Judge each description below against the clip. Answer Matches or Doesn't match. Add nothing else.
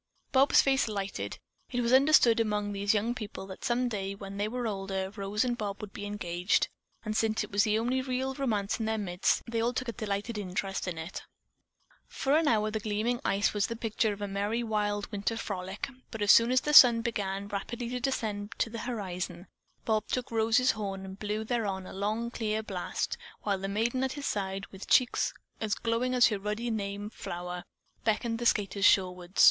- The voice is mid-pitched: Doesn't match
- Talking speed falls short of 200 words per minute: Doesn't match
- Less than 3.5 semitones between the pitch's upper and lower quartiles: Matches